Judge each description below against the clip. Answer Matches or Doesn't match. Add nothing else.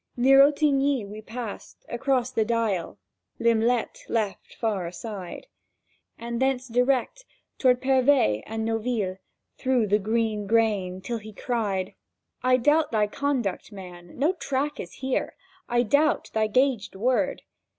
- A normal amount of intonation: Matches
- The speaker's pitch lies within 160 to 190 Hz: Doesn't match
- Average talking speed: Doesn't match